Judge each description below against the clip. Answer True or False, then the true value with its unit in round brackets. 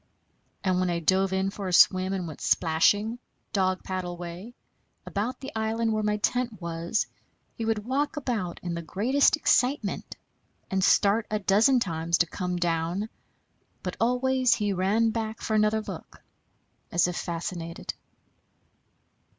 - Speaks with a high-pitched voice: True (200 Hz)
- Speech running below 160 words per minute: True (150 wpm)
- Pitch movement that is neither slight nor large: True (4.2 semitones)